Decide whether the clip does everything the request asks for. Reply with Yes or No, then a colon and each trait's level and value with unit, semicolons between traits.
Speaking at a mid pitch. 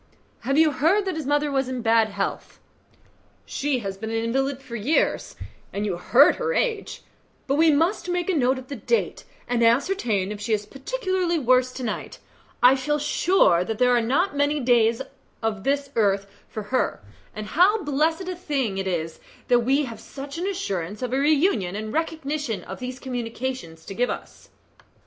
No: very high, 260 Hz